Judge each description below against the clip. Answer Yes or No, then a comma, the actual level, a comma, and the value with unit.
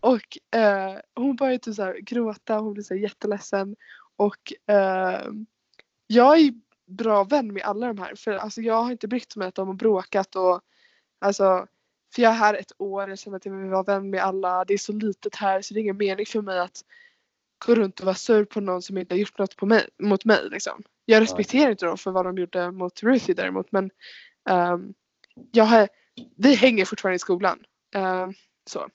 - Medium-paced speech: No, fast, 205 wpm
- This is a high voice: Yes, high, 205 Hz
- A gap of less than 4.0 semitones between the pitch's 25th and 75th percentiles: Yes, average, 3.0 semitones